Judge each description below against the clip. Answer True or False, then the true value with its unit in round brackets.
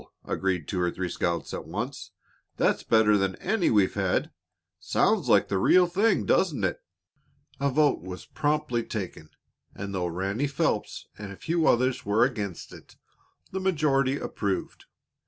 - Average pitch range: False (7.7 semitones)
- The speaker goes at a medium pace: True (155 wpm)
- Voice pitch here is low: True (110 Hz)